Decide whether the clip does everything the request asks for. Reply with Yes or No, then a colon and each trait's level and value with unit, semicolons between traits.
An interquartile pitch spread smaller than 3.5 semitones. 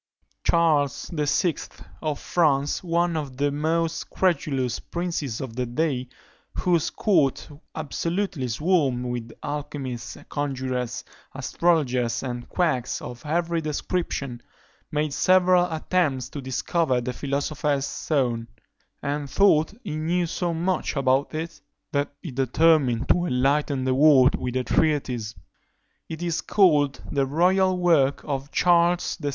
No: average, 4.3 semitones